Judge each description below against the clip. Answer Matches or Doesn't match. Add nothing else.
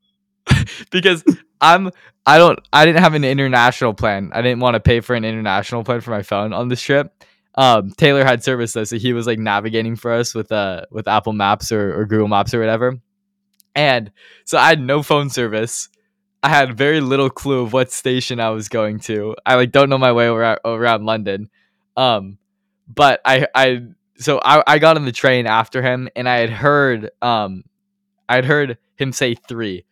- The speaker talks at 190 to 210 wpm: Matches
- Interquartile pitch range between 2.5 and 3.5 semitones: Doesn't match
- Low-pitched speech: Matches